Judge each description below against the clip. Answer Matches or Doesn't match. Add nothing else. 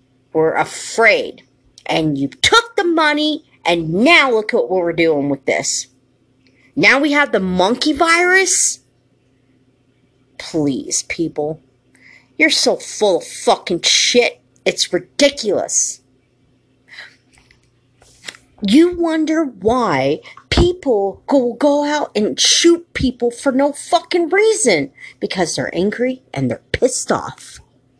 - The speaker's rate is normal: Doesn't match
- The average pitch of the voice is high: Matches